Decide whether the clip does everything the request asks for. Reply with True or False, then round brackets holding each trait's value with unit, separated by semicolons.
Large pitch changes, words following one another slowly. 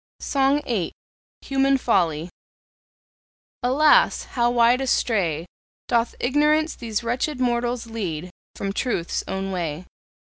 True (5.7 semitones; 105 wpm)